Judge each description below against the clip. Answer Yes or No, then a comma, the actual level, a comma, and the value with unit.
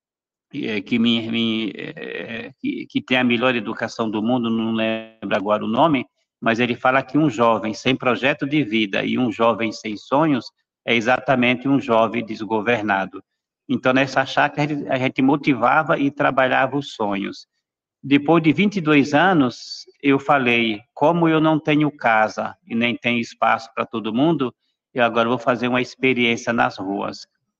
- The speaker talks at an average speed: Yes, average, 150 wpm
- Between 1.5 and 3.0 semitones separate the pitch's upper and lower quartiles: No, average, 3.7 semitones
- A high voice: No, low, 120 Hz